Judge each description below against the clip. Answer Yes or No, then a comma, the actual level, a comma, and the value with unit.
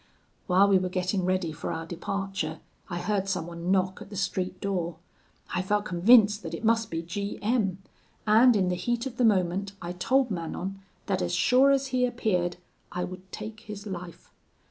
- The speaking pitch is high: Yes, high, 195 Hz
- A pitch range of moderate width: Yes, average, 3.1 semitones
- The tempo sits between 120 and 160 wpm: No, average, 190 wpm